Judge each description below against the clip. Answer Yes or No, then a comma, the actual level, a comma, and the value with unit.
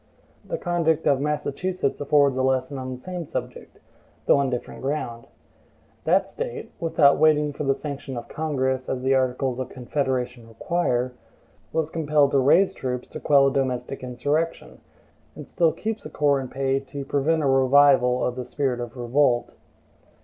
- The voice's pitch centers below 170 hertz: Yes, low, 135 Hz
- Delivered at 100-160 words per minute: No, average, 170 wpm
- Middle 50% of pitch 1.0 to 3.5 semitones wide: Yes, average, 2.7 semitones